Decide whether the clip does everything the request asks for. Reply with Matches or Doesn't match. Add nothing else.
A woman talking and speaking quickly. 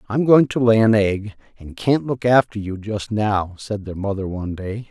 Doesn't match